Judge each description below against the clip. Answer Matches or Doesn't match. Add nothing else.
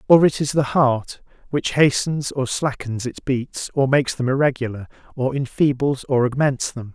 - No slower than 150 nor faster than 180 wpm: Matches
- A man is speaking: Matches